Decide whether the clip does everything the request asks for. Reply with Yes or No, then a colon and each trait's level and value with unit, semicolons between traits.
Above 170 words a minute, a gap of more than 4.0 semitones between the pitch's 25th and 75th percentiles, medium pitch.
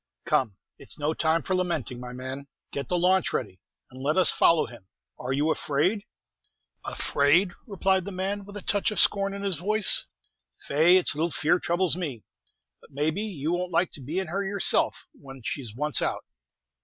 Yes: average, 190 wpm; average, 5.2 semitones; medium, 170 Hz